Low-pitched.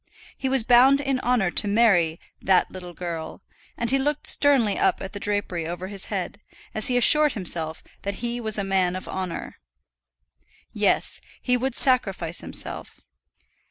No: high, 205 Hz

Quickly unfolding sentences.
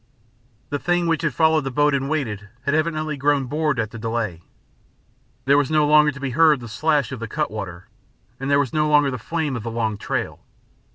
Yes: fast, 220 wpm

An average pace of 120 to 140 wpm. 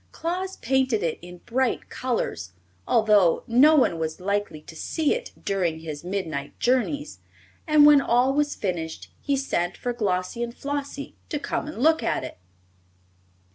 No: average, 155 wpm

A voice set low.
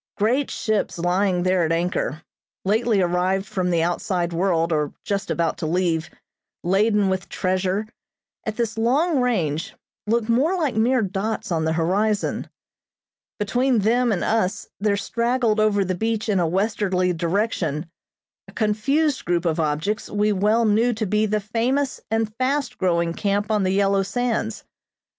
No: high, 200 Hz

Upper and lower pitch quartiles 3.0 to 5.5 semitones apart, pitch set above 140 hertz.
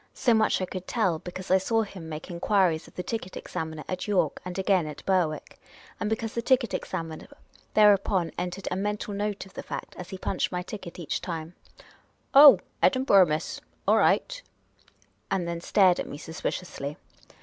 Yes: average, 3.4 semitones; medium, 185 Hz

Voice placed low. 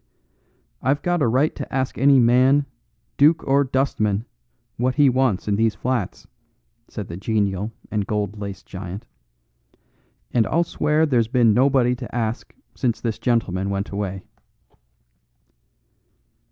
Yes: low, 120 Hz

